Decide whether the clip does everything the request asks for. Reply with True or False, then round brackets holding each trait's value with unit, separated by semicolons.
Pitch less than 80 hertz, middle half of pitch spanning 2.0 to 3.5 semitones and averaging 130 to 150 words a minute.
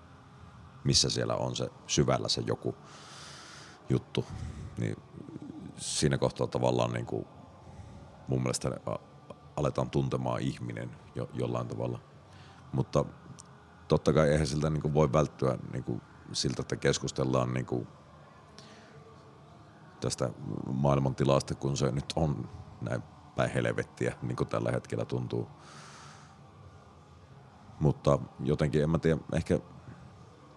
False (65 Hz; 2.8 semitones; 110 wpm)